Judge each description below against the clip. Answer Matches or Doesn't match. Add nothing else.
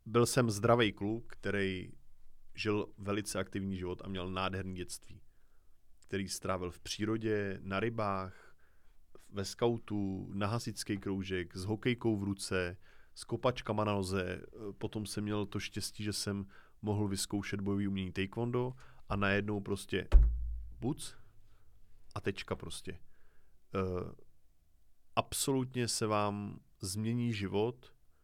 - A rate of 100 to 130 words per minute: Matches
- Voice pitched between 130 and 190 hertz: Doesn't match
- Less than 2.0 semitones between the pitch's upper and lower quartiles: Doesn't match